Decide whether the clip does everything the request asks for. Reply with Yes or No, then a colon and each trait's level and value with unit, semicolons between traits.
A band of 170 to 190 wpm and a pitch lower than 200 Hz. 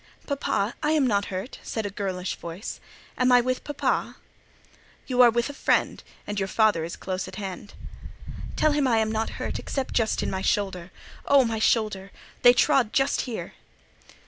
No: average, 180 wpm; high, 220 Hz